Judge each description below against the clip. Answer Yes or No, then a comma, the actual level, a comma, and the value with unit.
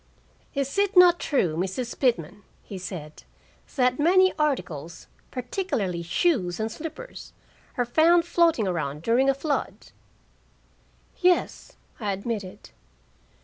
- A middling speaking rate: No, slow, 110 wpm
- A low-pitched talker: No, very high, 250 Hz